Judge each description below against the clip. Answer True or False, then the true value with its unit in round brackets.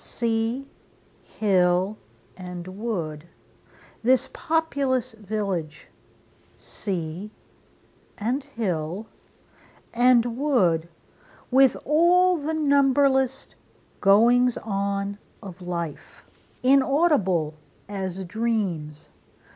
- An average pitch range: False (6.5 semitones)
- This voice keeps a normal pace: False (70 wpm)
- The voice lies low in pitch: False (220 Hz)